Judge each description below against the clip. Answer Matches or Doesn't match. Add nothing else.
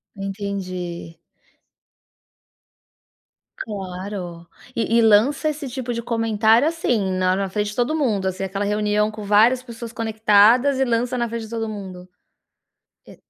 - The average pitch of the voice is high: Matches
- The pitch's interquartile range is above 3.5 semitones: Doesn't match